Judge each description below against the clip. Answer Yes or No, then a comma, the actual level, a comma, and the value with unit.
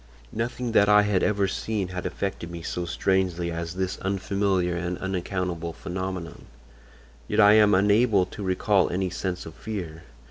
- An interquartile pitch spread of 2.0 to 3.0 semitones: Yes, narrow, 2.5 semitones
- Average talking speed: Yes, average, 155 wpm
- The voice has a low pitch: Yes, very low, 95 Hz